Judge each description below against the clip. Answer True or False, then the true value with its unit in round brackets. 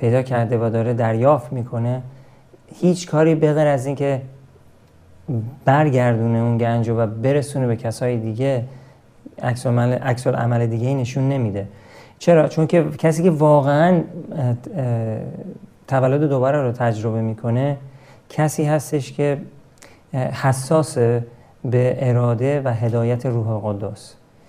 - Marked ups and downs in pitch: False (3.3 semitones)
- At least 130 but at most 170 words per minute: False (115 wpm)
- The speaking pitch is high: False (130 Hz)